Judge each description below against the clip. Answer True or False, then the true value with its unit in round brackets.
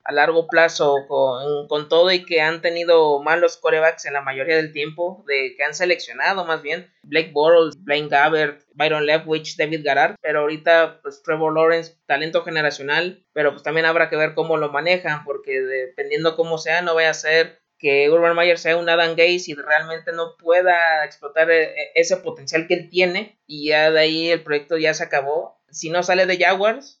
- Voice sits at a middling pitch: True (160 Hz)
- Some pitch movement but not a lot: False (2.1 semitones)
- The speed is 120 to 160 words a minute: False (190 wpm)